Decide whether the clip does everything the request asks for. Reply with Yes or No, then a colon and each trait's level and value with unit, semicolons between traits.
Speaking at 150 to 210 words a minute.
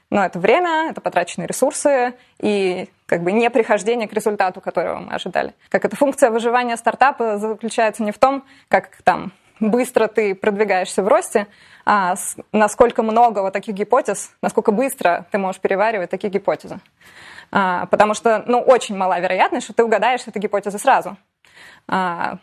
Yes: fast, 160 wpm